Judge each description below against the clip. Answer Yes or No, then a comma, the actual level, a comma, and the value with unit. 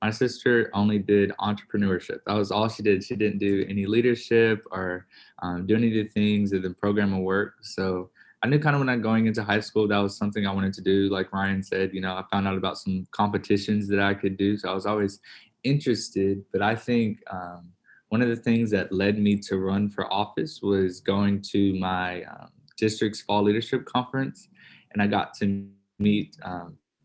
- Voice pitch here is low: Yes, low, 100 Hz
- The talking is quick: Yes, fast, 210 wpm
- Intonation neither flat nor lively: No, narrow, 2.0 semitones